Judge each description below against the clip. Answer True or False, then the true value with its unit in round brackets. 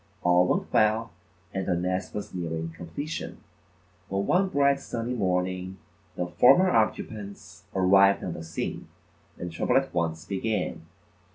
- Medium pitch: False (95 Hz)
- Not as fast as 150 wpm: True (140 wpm)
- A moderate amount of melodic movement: True (4.2 semitones)